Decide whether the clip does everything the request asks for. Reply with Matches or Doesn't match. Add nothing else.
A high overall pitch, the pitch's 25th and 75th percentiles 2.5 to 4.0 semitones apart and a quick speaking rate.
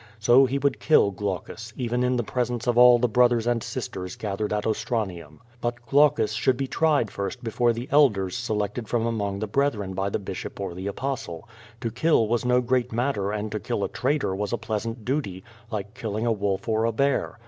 Doesn't match